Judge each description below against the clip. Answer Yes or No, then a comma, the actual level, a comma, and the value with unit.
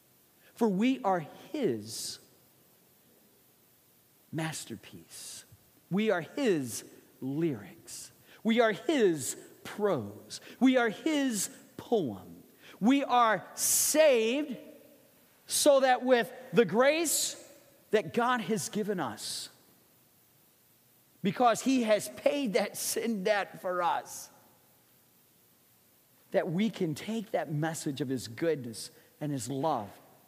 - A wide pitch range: Yes, wide, 8.1 semitones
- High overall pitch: Yes, high, 215 Hz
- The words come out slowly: Yes, slow, 100 wpm